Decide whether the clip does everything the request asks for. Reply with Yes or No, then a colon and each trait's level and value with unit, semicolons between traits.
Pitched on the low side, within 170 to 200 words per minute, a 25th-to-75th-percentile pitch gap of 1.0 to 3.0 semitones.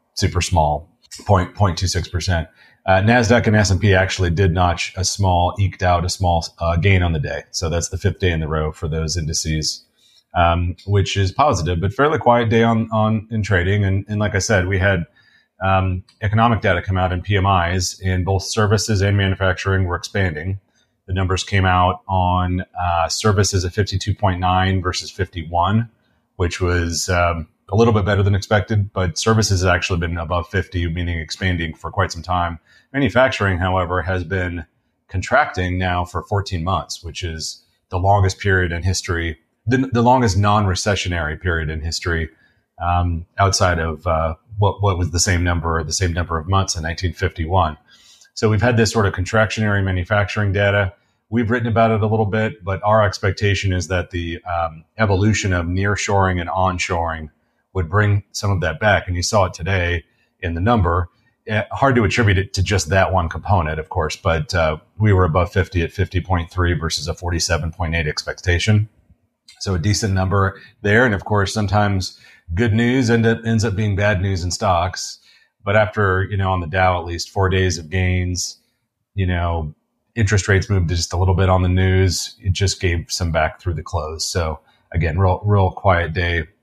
Yes: very low, 95 Hz; average, 185 wpm; average, 2.7 semitones